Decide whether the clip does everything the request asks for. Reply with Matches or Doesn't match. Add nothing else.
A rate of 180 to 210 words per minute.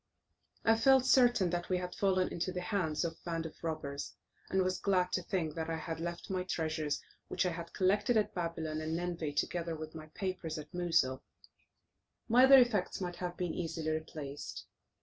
Matches